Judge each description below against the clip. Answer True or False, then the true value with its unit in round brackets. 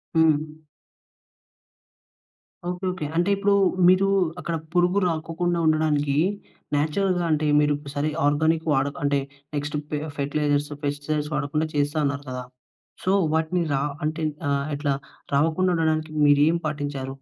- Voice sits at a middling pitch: True (155 Hz)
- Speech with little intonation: True (2.2 semitones)